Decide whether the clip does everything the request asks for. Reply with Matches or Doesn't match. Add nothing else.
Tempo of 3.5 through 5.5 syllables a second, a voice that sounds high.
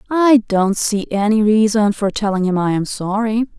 Matches